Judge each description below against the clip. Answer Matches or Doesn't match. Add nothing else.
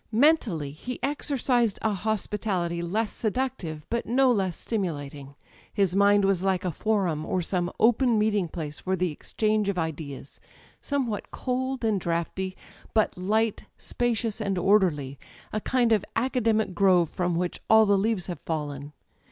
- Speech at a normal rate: Matches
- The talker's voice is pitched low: Doesn't match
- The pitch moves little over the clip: Doesn't match